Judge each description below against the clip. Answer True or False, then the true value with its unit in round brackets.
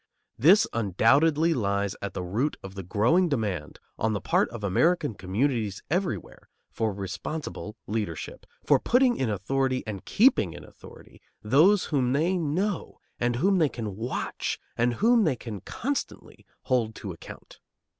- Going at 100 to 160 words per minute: True (150 wpm)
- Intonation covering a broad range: True (7.9 semitones)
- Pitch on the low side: True (120 Hz)